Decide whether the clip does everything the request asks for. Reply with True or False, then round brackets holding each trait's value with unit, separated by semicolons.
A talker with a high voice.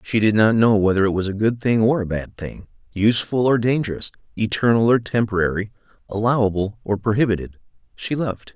False (110 Hz)